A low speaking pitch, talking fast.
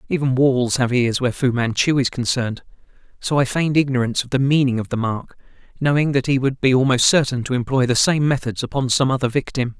Yes: low, 130 Hz; fast, 215 wpm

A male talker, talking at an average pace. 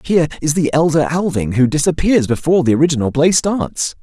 Yes: male; average, 180 wpm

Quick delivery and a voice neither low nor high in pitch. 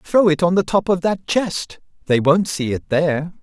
Yes: fast, 230 wpm; medium, 170 Hz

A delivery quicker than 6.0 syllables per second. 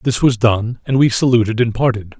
No: 5.2 syllables/s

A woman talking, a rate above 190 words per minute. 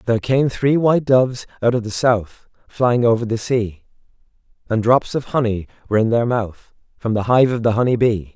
No: male; average, 200 wpm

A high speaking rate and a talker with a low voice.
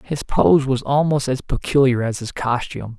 No: average, 180 wpm; low, 130 Hz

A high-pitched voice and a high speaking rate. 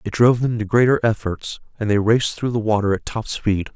No: low, 110 Hz; fast, 240 wpm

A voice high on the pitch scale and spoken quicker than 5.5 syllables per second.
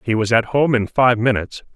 No: low, 120 Hz; 5.7 syllables/s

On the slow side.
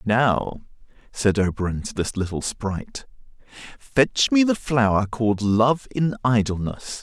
Yes: slow, 130 wpm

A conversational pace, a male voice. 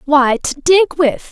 No: average, 180 wpm; female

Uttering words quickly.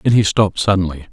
Yes: fast, 215 wpm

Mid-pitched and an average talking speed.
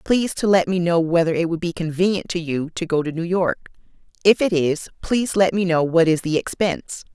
No: medium, 175 Hz; fast, 235 wpm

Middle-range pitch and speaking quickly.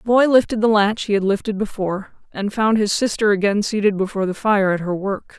No: high, 205 Hz; fast, 235 wpm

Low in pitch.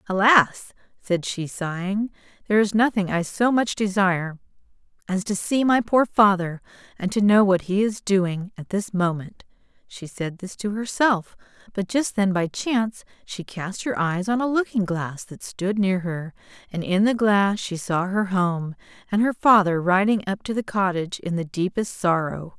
No: high, 195 Hz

